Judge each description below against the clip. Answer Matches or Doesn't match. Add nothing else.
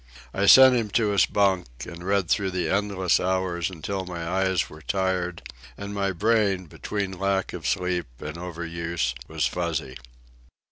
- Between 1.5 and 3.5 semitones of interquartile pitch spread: Matches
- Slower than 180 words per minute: Matches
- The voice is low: Matches